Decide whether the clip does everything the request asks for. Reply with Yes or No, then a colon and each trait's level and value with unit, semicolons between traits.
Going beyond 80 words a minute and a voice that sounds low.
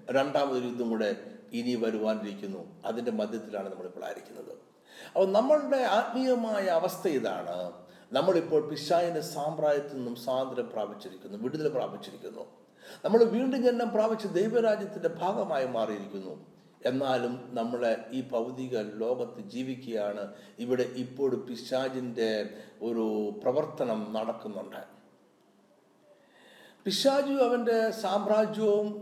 Yes: average, 90 wpm; low, 130 Hz